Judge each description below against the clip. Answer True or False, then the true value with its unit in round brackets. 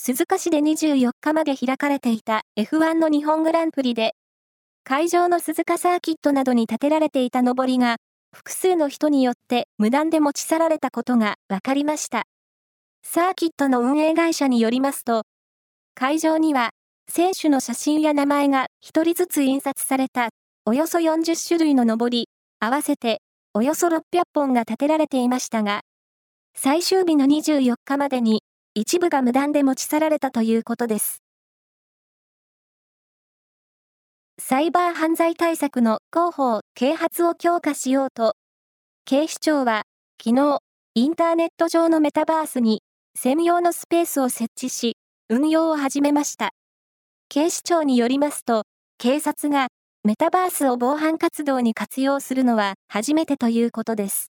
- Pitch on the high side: True (280 Hz)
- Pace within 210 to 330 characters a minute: True (295 characters per minute)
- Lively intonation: False (4.6 semitones)